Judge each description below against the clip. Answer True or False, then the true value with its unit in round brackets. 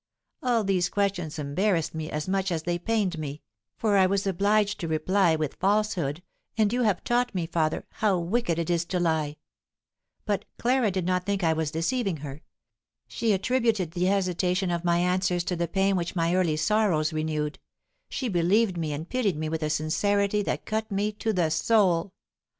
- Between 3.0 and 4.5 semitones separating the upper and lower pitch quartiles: True (4.0 semitones)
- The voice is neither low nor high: True (180 Hz)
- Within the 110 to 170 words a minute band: False (185 wpm)